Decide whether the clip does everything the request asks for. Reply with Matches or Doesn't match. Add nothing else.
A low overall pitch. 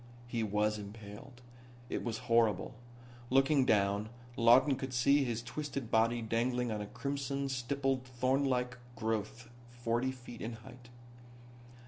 Matches